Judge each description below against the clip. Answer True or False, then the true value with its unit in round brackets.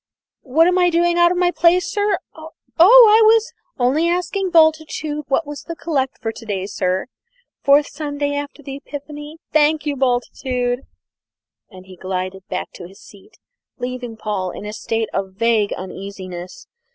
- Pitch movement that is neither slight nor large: False (7.6 semitones)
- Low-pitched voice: False (285 Hz)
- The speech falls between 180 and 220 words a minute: False (165 wpm)